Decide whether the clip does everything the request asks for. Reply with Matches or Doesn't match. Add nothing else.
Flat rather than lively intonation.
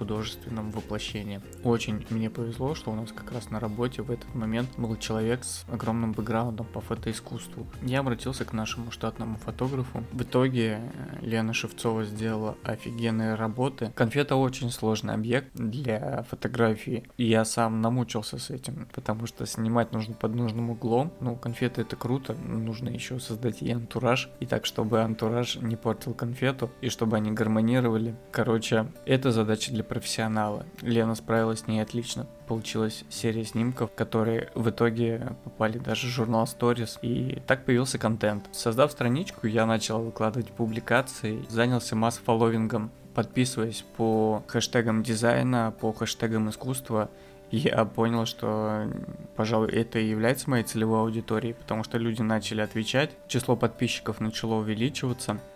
Matches